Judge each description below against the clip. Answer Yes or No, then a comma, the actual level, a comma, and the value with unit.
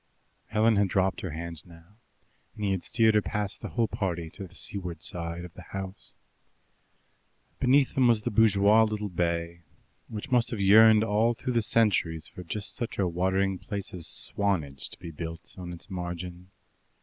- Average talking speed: Yes, average, 180 wpm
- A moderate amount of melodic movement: Yes, average, 3.8 semitones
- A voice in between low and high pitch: No, very low, 95 Hz